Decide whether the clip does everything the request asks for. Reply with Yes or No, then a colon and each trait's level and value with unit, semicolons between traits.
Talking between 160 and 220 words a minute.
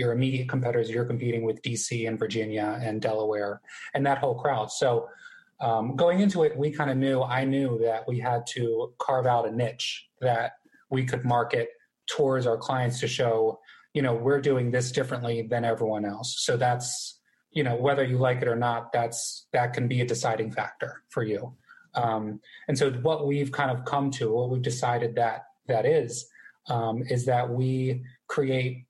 Yes: average, 190 wpm